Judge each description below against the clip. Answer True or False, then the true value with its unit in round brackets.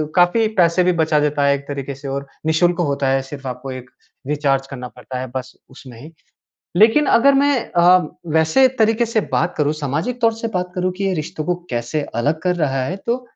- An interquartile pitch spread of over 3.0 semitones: True (5.1 semitones)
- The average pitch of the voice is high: False (155 Hz)